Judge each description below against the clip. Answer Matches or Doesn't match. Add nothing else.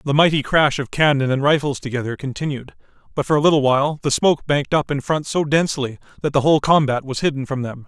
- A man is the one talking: Matches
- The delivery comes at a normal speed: Doesn't match